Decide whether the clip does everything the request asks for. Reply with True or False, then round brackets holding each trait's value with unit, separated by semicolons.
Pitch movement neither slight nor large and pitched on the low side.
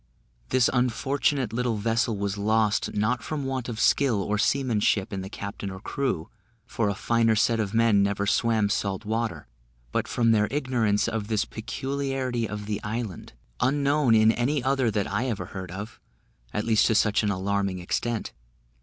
True (3.2 semitones; 110 Hz)